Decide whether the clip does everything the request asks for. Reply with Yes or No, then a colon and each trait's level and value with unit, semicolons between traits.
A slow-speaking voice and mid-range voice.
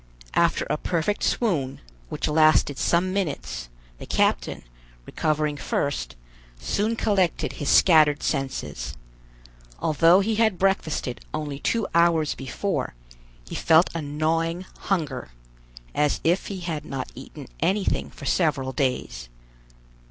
Yes: slow, 120 wpm; medium, 155 Hz